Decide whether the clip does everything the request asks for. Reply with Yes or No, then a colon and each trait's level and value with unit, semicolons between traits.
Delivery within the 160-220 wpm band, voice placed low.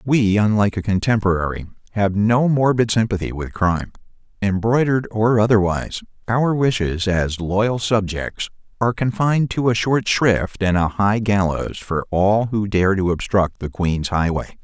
No: average, 150 wpm; low, 105 Hz